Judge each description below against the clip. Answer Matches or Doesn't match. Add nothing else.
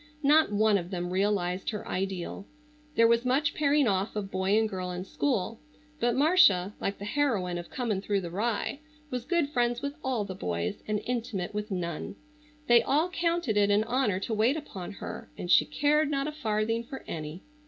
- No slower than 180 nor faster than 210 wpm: Matches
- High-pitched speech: Matches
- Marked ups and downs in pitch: Matches